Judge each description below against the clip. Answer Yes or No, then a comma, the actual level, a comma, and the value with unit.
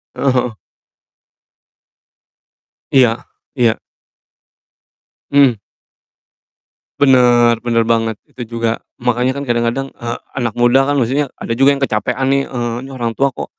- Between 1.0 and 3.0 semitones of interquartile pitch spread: Yes, narrow, 2.5 semitones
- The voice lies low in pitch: Yes, low, 120 Hz